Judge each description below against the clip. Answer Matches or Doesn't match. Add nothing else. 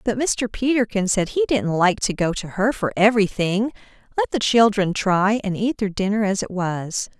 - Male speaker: Doesn't match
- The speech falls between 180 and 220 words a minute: Matches